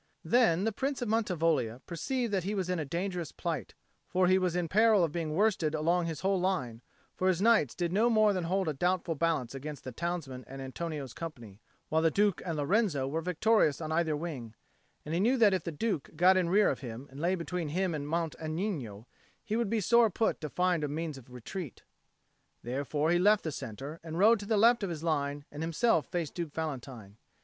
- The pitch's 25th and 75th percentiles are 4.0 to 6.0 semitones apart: Yes, average, 4.5 semitones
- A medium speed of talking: No, fast, 225 wpm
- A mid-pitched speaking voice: Yes, medium, 170 Hz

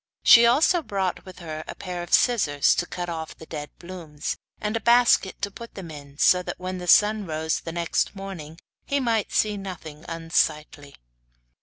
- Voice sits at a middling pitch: Yes, medium, 180 Hz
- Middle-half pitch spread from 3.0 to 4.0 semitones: No, average, 4.5 semitones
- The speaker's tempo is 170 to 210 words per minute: Yes, average, 180 wpm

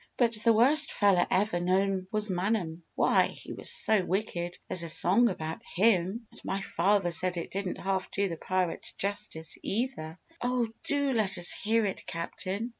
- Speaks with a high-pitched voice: Yes, high, 195 Hz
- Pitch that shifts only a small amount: No, average, 3.9 semitones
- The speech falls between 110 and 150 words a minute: No, average, 175 wpm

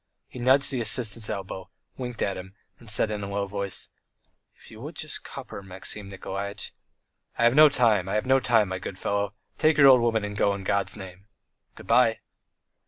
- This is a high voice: No, low, 105 Hz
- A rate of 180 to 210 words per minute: Yes, average, 200 wpm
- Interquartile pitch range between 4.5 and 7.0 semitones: No, average, 3.5 semitones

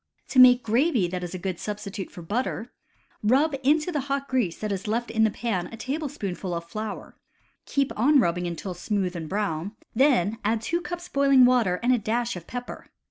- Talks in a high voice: Yes, high, 220 Hz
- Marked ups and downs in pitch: Yes, wide, 5.8 semitones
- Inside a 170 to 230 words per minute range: Yes, average, 200 wpm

